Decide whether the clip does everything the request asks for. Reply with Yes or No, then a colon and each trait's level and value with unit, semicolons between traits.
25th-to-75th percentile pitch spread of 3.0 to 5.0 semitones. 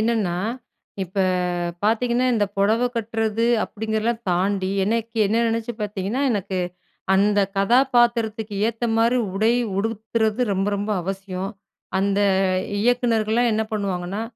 No: narrow, 2.6 semitones